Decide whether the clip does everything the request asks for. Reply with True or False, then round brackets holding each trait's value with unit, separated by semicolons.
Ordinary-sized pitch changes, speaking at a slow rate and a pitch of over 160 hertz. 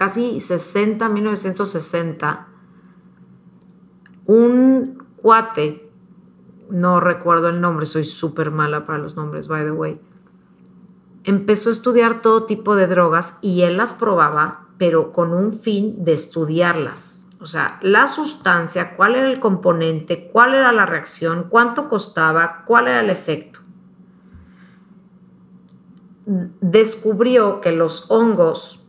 True (4.1 semitones; 120 wpm; 185 Hz)